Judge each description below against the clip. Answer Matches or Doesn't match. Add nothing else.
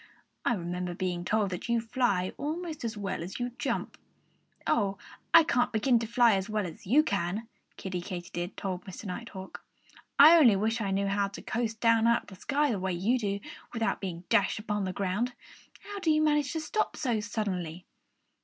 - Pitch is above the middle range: Matches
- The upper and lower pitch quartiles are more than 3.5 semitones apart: Matches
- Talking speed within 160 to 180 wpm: Doesn't match